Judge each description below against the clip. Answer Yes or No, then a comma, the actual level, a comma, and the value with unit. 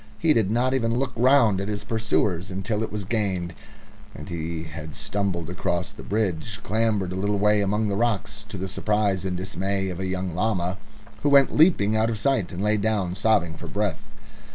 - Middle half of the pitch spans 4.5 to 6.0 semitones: No, average, 3.2 semitones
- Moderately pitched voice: No, low, 100 Hz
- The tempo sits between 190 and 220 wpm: Yes, average, 200 wpm